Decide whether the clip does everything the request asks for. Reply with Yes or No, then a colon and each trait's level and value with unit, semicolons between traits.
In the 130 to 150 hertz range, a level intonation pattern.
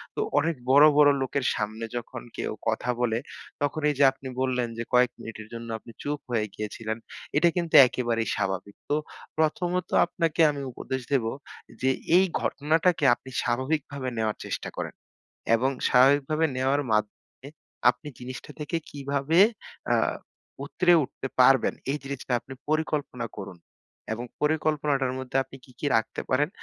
No: low, 135 Hz; average, 3.8 semitones